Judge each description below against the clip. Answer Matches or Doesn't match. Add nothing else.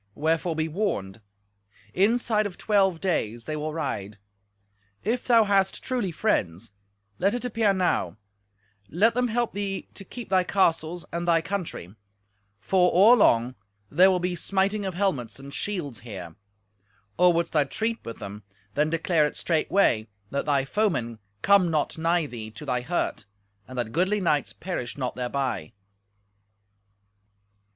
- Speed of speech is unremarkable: Matches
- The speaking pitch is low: Doesn't match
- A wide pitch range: Matches